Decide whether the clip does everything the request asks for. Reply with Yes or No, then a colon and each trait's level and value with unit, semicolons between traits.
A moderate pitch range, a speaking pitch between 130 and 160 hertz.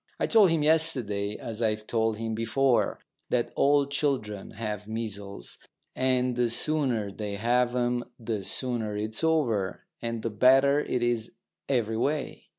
No: average, 3.8 semitones; low, 120 Hz